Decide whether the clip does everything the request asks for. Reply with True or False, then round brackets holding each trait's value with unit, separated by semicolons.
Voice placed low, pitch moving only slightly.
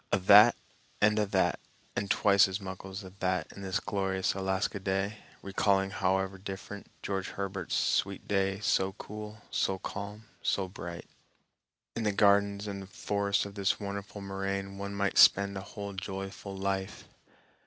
True (100 Hz; 1.0 semitones)